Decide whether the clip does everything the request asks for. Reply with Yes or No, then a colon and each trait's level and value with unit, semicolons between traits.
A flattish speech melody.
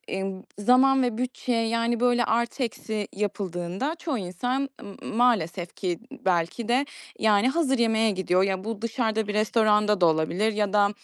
No: average, 3.9 semitones